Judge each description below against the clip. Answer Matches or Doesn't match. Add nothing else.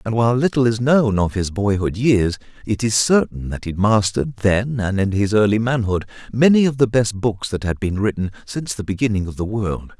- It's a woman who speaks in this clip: Doesn't match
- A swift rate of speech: Matches